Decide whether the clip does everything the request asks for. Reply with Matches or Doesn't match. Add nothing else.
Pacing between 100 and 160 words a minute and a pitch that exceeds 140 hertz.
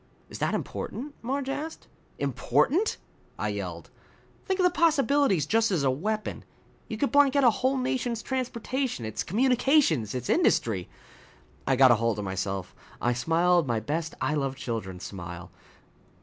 Matches